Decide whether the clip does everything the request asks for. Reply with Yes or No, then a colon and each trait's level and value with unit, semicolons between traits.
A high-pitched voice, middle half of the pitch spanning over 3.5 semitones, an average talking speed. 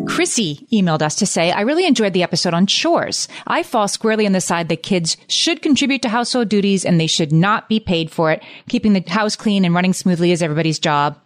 No: high, 195 Hz; average, 4.9 semitones; fast, 230 wpm